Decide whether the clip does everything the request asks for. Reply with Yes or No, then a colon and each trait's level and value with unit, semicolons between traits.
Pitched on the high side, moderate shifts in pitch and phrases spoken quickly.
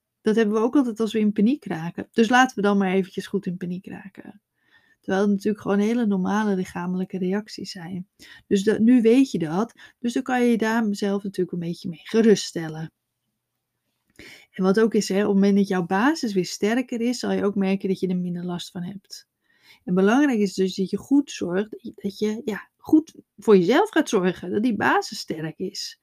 Yes: high, 200 Hz; average, 3.4 semitones; fast, 210 wpm